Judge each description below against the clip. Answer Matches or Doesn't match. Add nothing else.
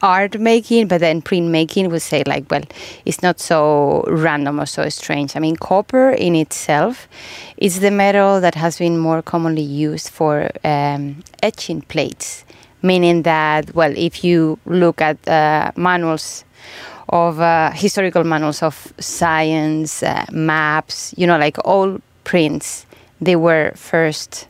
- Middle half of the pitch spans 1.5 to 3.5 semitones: Matches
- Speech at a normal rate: Matches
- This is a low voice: Doesn't match